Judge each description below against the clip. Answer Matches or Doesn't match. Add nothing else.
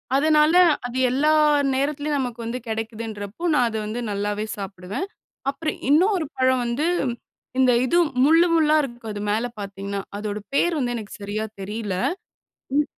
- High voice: Matches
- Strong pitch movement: Matches